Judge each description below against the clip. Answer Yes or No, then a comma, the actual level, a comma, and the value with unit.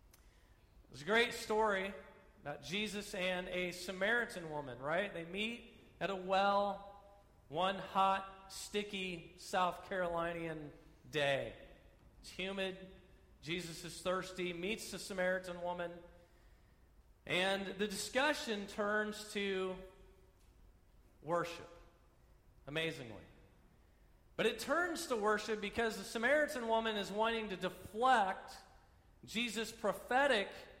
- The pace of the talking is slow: Yes, slow, 105 wpm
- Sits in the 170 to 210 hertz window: Yes, high, 190 Hz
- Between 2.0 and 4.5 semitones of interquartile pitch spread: Yes, average, 3.8 semitones